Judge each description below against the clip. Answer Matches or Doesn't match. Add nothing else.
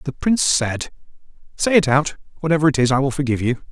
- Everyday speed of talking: Doesn't match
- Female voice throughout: Doesn't match